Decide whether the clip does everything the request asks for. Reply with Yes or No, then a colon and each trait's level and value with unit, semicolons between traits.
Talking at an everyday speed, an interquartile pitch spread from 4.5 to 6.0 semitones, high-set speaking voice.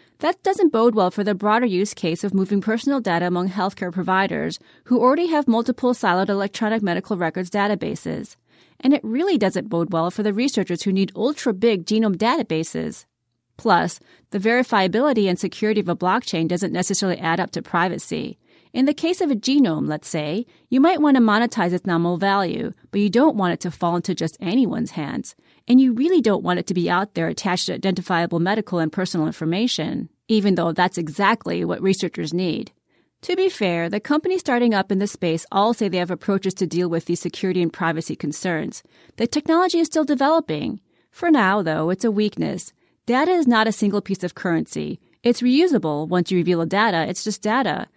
Yes: average, 195 wpm; average, 5.2 semitones; high, 200 Hz